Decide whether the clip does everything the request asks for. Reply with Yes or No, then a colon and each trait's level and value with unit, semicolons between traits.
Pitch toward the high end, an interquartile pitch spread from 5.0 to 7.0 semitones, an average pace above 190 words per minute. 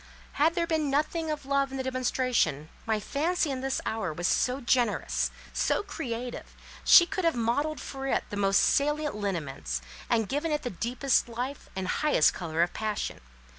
No: very high, 255 Hz; wide, 5.6 semitones; average, 175 wpm